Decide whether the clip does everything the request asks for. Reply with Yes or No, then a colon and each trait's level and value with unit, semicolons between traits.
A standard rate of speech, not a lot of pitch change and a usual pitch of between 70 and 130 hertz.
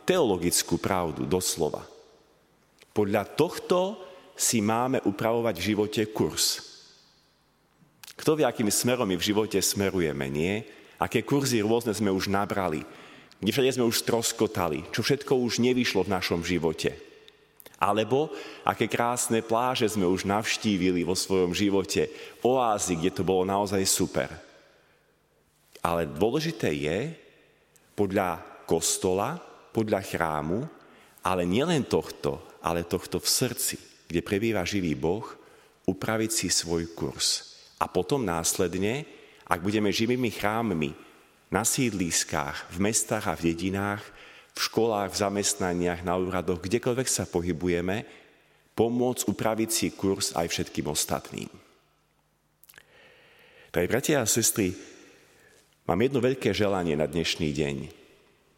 No: average, 120 wpm; average, 4.2 semitones; low, 105 Hz